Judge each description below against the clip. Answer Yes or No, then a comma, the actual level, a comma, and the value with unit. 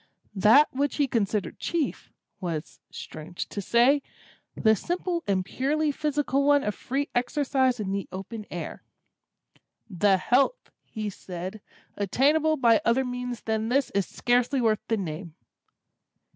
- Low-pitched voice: No, high, 240 Hz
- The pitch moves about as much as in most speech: No, wide, 5.9 semitones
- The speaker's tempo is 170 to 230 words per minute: No, slow, 135 wpm